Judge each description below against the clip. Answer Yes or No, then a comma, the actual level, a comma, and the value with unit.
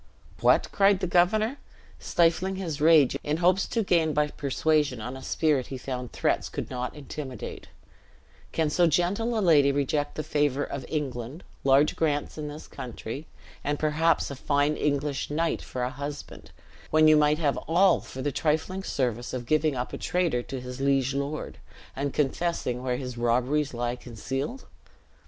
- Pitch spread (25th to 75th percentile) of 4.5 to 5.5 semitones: No, average, 3.6 semitones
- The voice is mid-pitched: Yes, medium, 145 Hz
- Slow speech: No, average, 170 wpm